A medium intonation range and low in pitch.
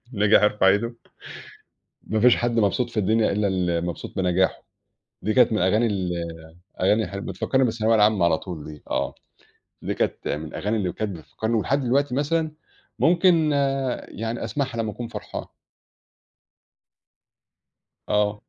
Yes: average, 4.0 semitones; low, 110 Hz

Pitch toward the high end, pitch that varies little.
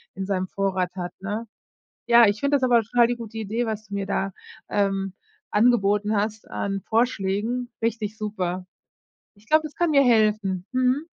No: high, 215 Hz; average, 3.3 semitones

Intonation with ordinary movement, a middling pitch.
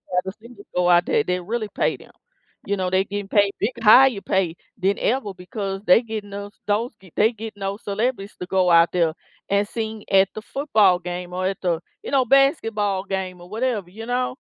No: average, 3.1 semitones; high, 200 Hz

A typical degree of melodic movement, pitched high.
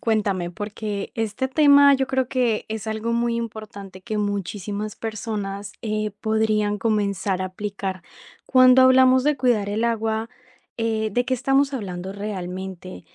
Yes: average, 3.0 semitones; high, 215 Hz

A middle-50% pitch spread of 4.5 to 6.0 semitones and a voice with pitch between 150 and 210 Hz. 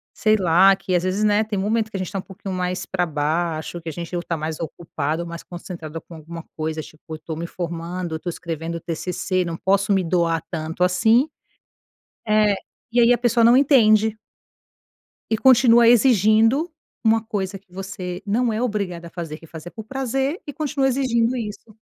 Yes: average, 4.8 semitones; high, 190 Hz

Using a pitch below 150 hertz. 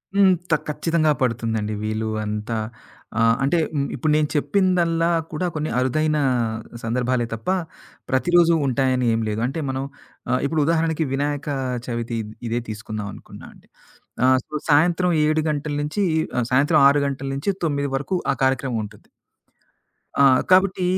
Yes: medium, 140 Hz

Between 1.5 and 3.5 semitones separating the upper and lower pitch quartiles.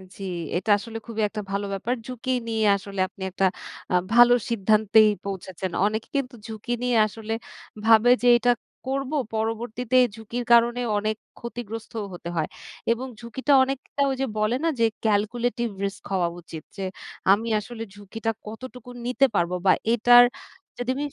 Yes: average, 2.8 semitones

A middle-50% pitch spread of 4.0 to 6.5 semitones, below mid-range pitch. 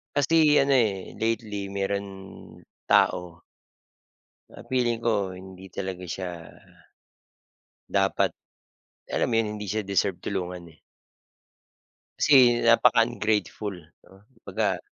No: average, 3.5 semitones; low, 100 Hz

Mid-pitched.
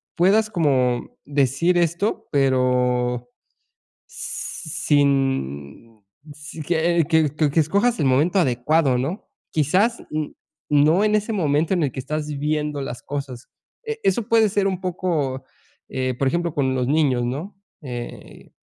Yes: medium, 150 Hz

